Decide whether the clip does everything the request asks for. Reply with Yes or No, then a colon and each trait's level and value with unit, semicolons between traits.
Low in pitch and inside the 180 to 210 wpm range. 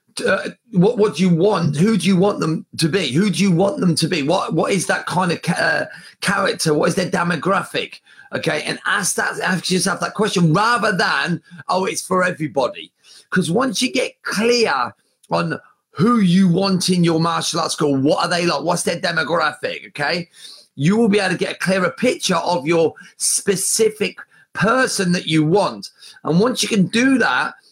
No: medium, 185 Hz; average, 195 wpm